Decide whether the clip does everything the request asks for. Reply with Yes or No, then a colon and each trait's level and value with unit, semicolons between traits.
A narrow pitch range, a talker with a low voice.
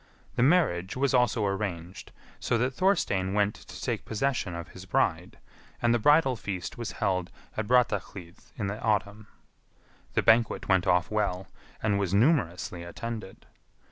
No: average, 4.3 semitones; low, 105 Hz